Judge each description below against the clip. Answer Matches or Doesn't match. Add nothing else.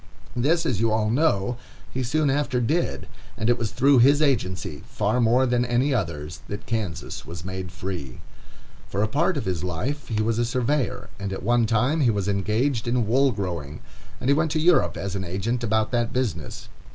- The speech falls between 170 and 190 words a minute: Doesn't match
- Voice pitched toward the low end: Matches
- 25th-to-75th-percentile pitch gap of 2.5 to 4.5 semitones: Doesn't match